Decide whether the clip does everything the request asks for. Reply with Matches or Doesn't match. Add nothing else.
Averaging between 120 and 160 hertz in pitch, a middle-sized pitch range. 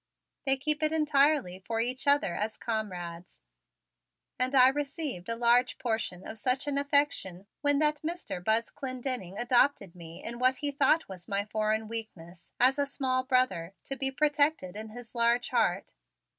Doesn't match